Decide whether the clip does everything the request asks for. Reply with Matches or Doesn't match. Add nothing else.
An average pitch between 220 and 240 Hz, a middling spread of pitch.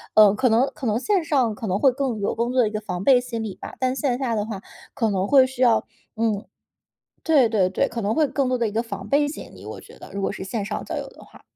Matches